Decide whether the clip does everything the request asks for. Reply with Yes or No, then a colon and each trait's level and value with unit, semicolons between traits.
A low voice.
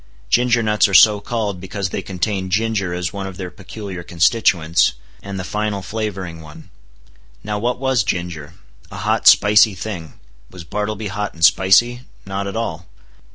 Yes: low, 100 Hz